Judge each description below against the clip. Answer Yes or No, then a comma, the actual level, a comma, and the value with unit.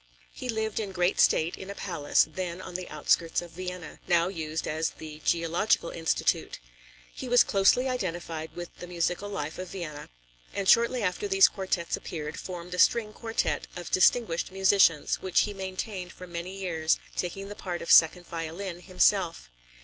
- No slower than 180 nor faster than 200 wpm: No, average, 170 wpm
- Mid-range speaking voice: Yes, medium, 180 Hz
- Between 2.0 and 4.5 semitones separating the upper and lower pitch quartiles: Yes, average, 2.7 semitones